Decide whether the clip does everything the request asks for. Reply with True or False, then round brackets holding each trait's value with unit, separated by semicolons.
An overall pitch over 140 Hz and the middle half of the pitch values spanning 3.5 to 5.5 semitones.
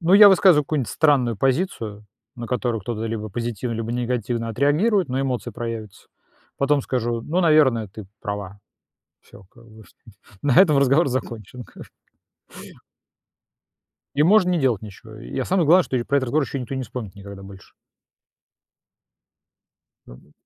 False (125 Hz; 4.9 semitones)